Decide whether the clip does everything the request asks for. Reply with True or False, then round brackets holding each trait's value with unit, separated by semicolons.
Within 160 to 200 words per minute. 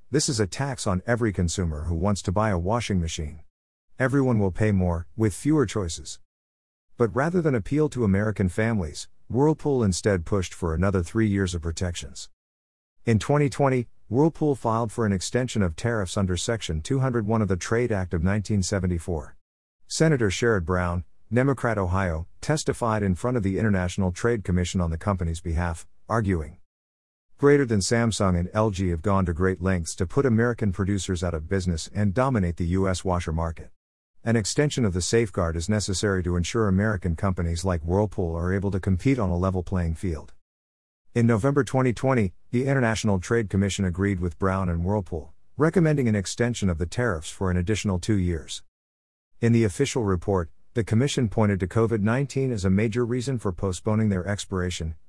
True (175 wpm)